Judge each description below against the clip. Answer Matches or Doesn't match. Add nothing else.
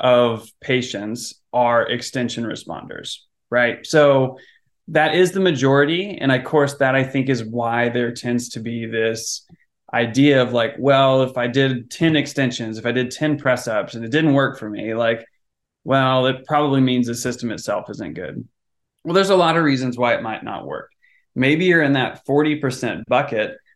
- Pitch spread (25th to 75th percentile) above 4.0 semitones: Doesn't match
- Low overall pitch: Matches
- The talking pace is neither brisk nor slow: Matches